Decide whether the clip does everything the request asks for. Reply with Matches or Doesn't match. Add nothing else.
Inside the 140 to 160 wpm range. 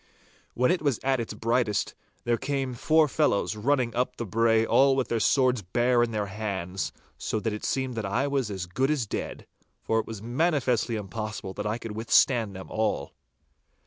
Doesn't match